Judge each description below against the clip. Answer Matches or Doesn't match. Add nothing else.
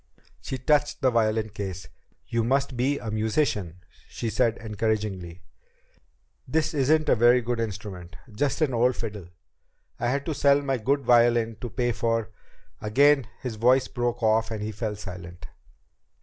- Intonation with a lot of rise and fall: Doesn't match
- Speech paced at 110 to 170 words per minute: Matches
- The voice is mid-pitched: Doesn't match